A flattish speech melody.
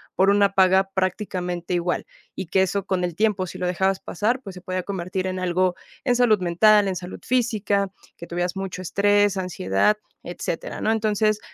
Yes: narrow, 2.2 semitones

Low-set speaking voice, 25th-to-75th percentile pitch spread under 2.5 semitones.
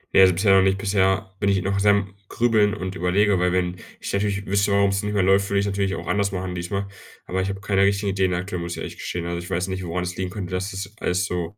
Yes: very low, 95 Hz; narrow, 1.7 semitones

